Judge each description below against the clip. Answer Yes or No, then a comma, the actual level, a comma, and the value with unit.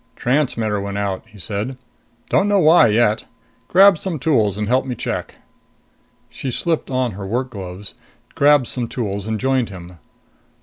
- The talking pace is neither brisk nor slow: Yes, average, 160 wpm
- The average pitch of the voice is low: Yes, low, 115 Hz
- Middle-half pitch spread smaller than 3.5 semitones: No, average, 4.7 semitones